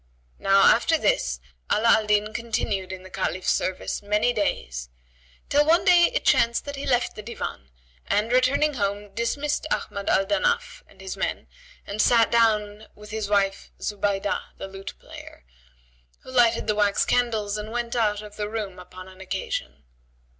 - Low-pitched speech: No, high, 210 Hz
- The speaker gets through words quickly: No, average, 170 wpm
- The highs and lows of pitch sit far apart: No, average, 3.1 semitones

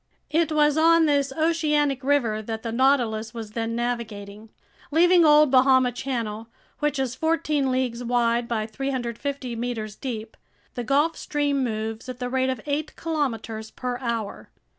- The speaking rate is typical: Yes, average, 150 wpm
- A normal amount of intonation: Yes, average, 4.1 semitones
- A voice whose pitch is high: Yes, very high, 255 Hz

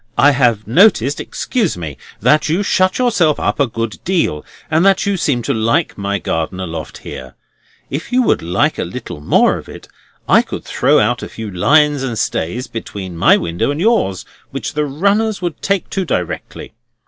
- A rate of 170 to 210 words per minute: Yes, average, 185 wpm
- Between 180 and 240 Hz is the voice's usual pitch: No, medium, 140 Hz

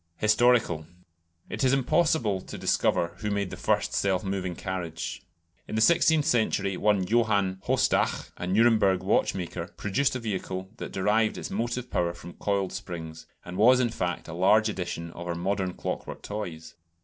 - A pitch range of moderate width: Yes, average, 4.0 semitones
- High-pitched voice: No, low, 100 Hz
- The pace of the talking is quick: No, average, 160 wpm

